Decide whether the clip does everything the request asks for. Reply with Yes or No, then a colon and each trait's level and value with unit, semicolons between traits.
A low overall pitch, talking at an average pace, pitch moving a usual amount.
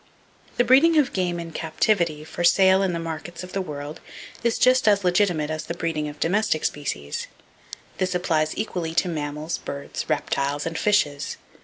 No: medium, 170 Hz; average, 170 wpm; average, 3.9 semitones